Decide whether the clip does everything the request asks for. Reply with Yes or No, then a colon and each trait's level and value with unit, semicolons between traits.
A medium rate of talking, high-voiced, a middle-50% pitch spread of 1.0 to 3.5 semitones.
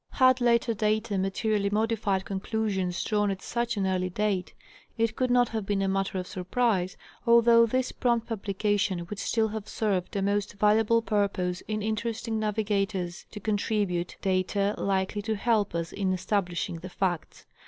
Yes: average, 160 wpm; high, 205 Hz; narrow, 2.6 semitones